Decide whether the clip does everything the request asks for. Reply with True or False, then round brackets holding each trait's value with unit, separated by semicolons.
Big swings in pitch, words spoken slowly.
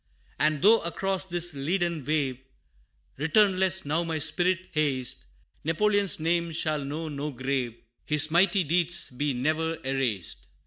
False (3.8 semitones; 130 wpm)